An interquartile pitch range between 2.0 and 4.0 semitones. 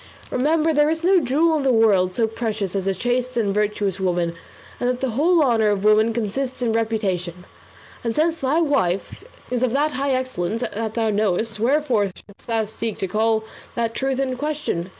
No: average, 4.5 semitones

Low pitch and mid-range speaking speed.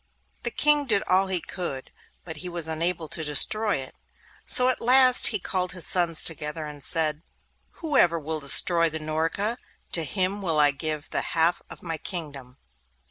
No: medium, 165 Hz; average, 175 wpm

